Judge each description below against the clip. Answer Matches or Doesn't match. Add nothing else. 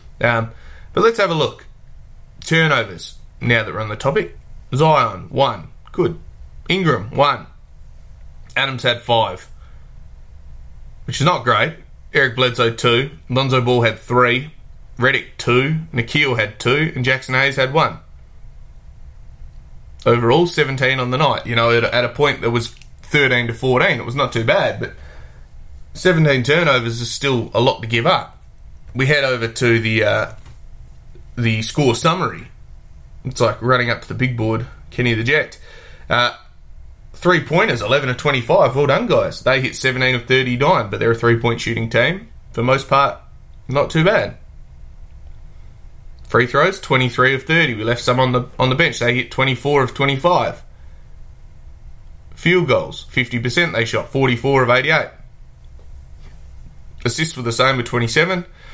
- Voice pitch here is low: Matches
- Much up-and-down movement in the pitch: Doesn't match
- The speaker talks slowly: Doesn't match